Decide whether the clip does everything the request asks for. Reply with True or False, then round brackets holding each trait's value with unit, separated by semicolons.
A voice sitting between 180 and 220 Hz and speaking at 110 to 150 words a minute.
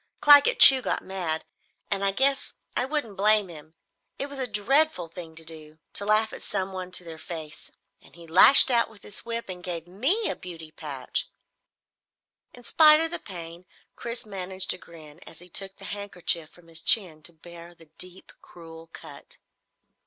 False (185 Hz; 180 wpm)